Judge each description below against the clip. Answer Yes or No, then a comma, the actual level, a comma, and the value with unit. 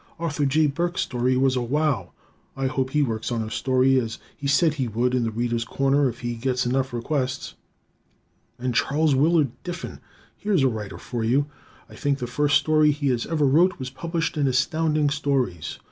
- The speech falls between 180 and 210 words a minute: Yes, average, 190 wpm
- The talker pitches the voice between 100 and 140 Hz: Yes, low, 135 Hz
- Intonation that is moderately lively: Yes, average, 3.5 semitones